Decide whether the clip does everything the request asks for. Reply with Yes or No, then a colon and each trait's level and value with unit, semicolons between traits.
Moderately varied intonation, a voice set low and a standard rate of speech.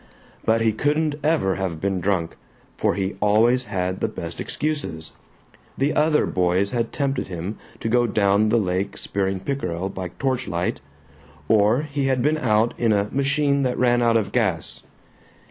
No: wide, 5.8 semitones; low, 110 Hz; average, 165 wpm